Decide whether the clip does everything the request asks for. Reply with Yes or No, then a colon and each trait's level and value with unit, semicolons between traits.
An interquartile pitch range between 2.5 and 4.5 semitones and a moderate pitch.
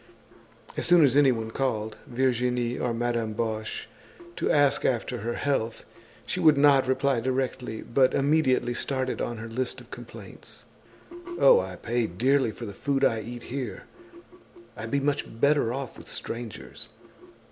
No: average, 3.1 semitones; low, 125 Hz